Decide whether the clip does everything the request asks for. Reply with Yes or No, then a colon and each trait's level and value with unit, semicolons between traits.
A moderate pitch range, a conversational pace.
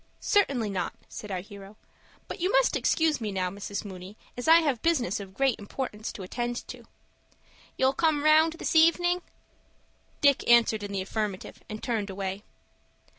No: wide, 7.5 semitones; average, 165 wpm